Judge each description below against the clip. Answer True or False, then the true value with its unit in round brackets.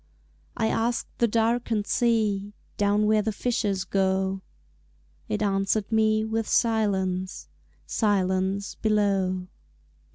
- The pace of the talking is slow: True (100 wpm)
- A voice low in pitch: False (205 Hz)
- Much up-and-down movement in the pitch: False (2.4 semitones)